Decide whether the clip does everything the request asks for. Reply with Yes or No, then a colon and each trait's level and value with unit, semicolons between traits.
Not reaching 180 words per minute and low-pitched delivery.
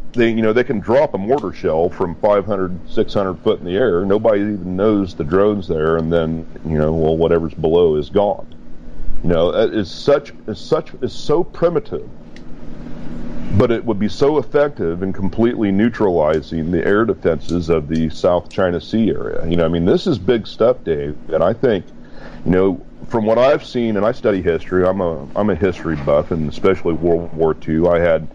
No: average, 200 wpm; very low, 85 Hz